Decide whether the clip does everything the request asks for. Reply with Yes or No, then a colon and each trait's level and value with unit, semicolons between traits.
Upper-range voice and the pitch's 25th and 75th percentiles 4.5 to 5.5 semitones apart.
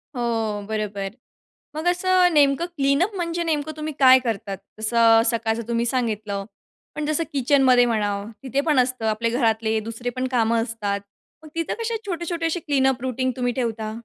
Yes: very high, 250 Hz; average, 5.0 semitones